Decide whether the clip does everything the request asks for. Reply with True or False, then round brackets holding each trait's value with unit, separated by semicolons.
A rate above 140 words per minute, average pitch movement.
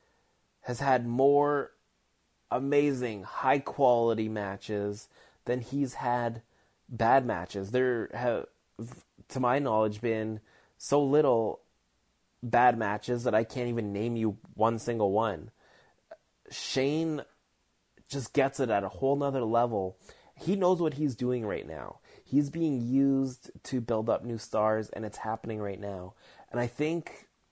False (135 wpm; 3.9 semitones)